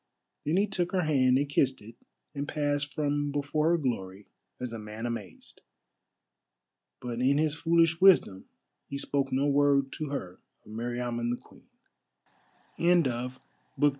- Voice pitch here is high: No, medium, 140 Hz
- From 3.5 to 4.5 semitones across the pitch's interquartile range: Yes, average, 3.9 semitones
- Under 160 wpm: Yes, average, 150 wpm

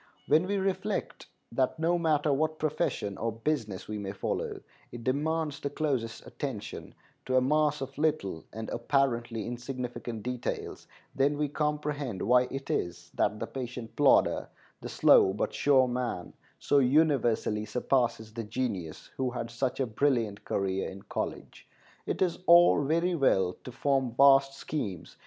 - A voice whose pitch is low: Yes, low, 130 Hz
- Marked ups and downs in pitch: No, average, 4.5 semitones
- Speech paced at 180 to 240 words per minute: No, average, 150 wpm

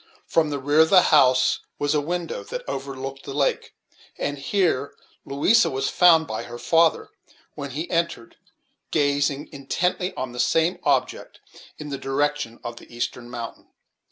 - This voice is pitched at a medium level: Yes, medium, 145 Hz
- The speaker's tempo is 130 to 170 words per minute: Yes, average, 155 wpm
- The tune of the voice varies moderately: Yes, average, 3.3 semitones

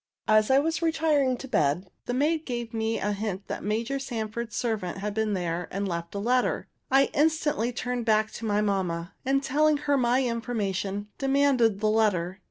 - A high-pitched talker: Yes, high, 225 Hz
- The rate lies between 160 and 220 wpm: Yes, average, 180 wpm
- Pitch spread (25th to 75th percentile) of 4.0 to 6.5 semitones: Yes, average, 5.0 semitones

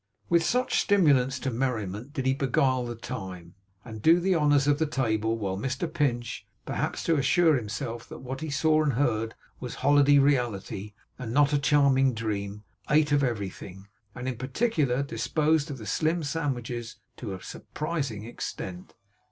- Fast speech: No, average, 165 wpm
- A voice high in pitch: No, low, 130 Hz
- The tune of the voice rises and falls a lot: No, average, 4.5 semitones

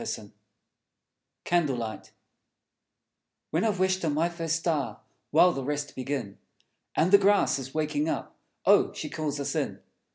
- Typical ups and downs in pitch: Yes, average, 3.7 semitones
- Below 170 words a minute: Yes, average, 150 wpm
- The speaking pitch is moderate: Yes, medium, 155 Hz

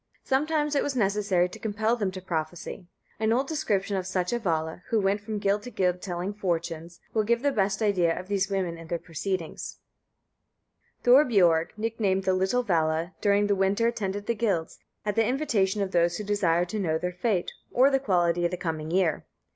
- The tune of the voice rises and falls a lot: No, average, 3.9 semitones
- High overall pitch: Yes, high, 195 Hz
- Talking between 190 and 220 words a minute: Yes, average, 195 wpm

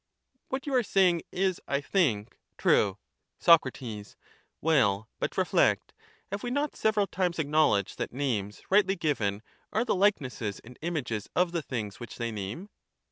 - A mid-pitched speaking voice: Yes, medium, 150 Hz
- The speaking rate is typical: Yes, average, 160 wpm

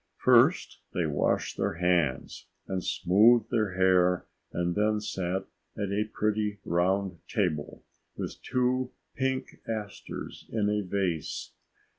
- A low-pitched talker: Yes, low, 100 Hz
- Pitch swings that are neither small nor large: Yes, average, 3.3 semitones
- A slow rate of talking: Yes, slow, 120 wpm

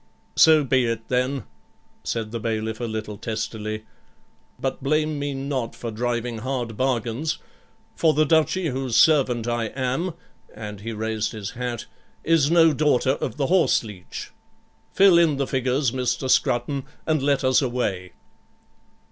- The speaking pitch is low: Yes, low, 125 Hz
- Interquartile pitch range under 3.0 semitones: No, average, 4.1 semitones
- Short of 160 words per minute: Yes, average, 150 wpm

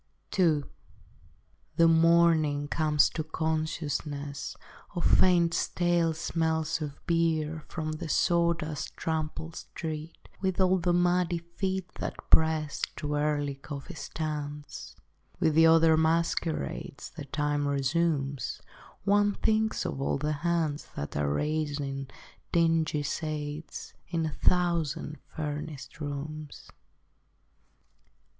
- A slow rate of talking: Yes, slow, 110 wpm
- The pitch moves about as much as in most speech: No, narrow, 2.3 semitones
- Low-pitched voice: No, medium, 155 Hz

